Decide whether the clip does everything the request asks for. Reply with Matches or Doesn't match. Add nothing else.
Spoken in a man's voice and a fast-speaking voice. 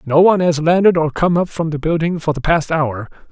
Matches